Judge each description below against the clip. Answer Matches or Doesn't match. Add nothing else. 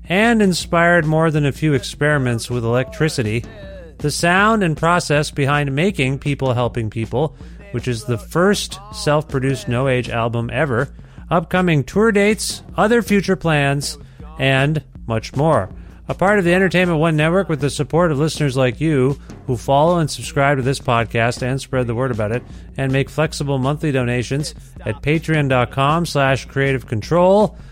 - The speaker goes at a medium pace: Matches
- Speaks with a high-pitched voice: Doesn't match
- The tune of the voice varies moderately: Matches